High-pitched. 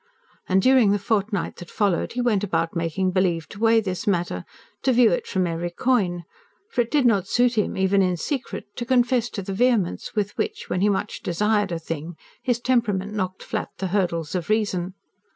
Yes: high, 200 Hz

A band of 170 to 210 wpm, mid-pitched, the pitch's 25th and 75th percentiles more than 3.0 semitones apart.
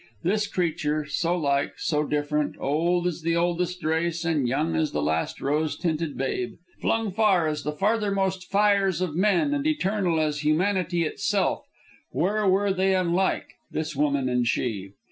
No: average, 160 wpm; medium, 170 Hz; average, 4.2 semitones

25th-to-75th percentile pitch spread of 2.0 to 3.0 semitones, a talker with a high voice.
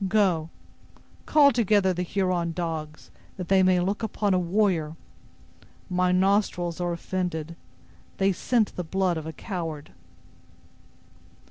No: narrow, 2.6 semitones; medium, 180 Hz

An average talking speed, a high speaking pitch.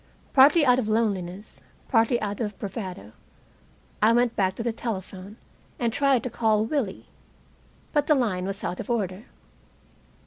Yes: average, 150 wpm; high, 220 Hz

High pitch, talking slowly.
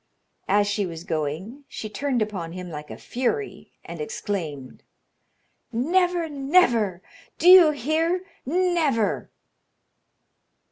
Yes: high, 240 Hz; slow, 105 wpm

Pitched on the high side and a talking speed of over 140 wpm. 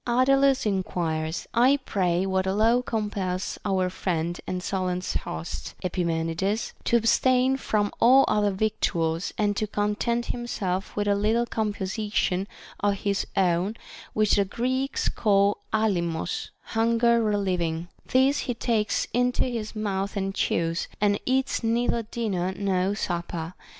No: high, 205 Hz; slow, 135 wpm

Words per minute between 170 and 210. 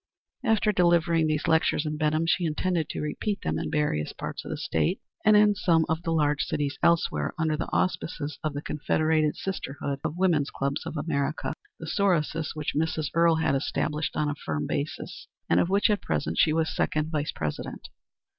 Yes: average, 190 wpm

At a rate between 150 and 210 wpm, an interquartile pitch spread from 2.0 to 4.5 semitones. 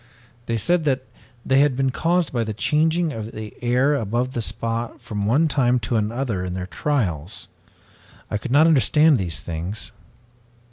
No: average, 180 wpm; average, 5.3 semitones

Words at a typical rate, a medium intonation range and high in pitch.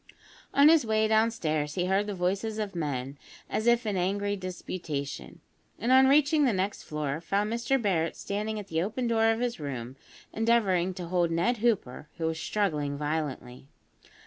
No: average, 170 wpm; wide, 5.7 semitones; high, 195 Hz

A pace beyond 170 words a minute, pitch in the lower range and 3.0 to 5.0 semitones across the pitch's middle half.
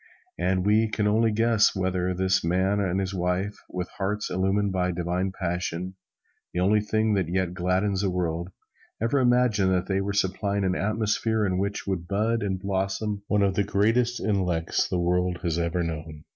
No: average, 180 wpm; very low, 95 Hz; narrow, 2.5 semitones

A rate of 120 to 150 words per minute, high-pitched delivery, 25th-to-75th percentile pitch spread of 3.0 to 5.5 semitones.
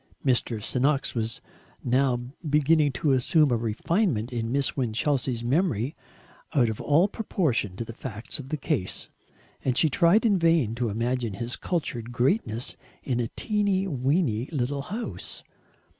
No: average, 145 wpm; low, 130 Hz; average, 4.8 semitones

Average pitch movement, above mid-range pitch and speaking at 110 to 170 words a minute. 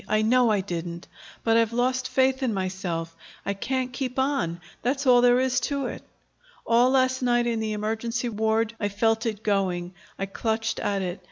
No: average, 4.0 semitones; high, 225 Hz; average, 185 wpm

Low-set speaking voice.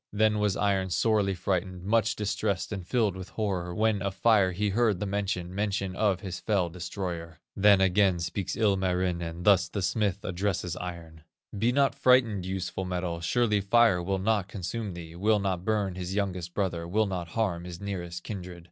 Yes: very low, 95 Hz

